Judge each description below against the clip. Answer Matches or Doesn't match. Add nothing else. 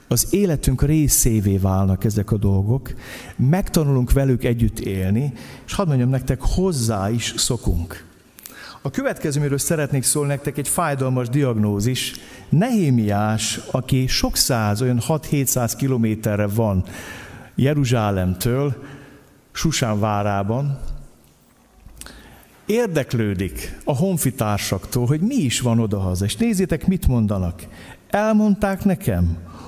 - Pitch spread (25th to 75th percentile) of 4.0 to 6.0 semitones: Matches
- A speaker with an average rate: Doesn't match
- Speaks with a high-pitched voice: Doesn't match